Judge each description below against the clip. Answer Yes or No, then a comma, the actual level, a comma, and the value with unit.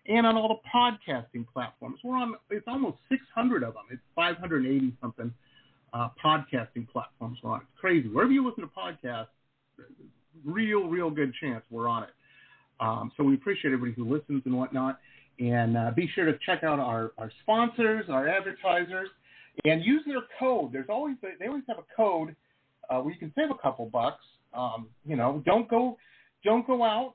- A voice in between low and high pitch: Yes, medium, 155 Hz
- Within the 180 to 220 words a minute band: Yes, average, 190 wpm